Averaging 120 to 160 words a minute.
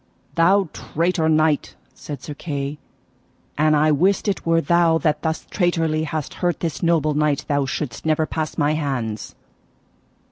Yes: average, 150 wpm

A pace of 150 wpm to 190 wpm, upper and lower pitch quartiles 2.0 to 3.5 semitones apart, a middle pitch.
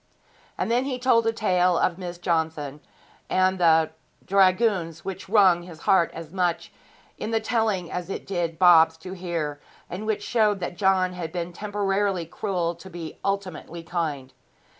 Yes: average, 165 wpm; average, 2.9 semitones; medium, 180 Hz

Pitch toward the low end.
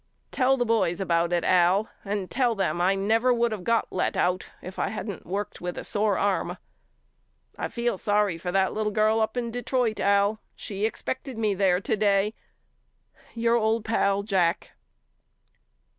No: high, 205 Hz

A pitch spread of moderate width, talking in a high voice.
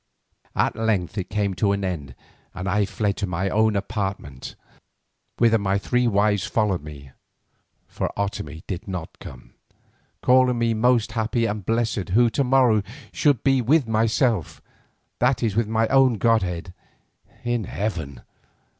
No: average, 3.5 semitones; low, 105 Hz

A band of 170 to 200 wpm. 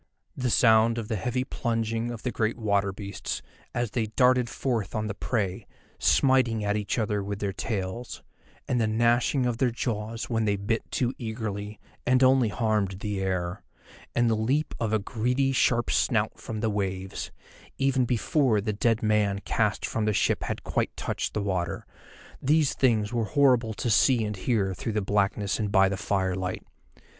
Yes: average, 175 wpm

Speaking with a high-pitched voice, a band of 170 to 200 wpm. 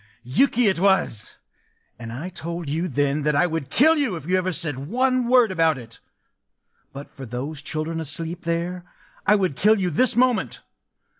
No: medium, 170 Hz; average, 175 wpm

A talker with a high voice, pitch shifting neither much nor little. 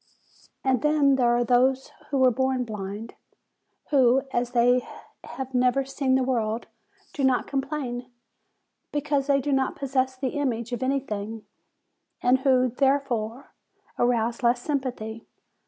No: very high, 255 Hz; narrow, 2.1 semitones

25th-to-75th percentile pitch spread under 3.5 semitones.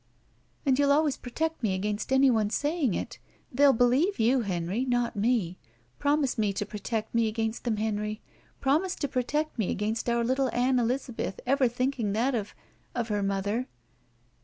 No: average, 4.0 semitones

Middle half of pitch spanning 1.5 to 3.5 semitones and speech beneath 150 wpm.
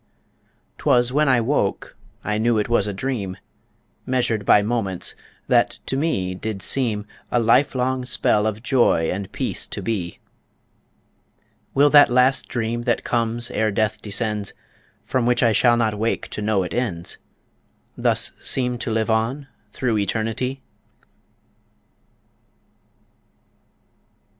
Yes: average, 3.1 semitones; slow, 135 wpm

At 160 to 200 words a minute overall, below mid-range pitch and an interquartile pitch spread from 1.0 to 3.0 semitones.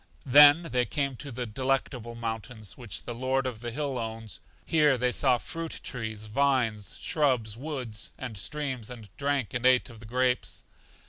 No: average, 170 wpm; low, 125 Hz; average, 3.4 semitones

